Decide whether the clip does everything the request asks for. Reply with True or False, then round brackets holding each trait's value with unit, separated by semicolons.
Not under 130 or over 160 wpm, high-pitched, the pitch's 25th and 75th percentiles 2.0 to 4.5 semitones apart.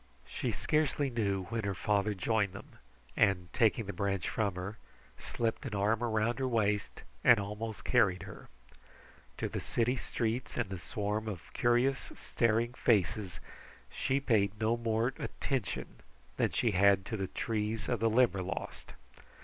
False (150 wpm; 110 Hz; 2.9 semitones)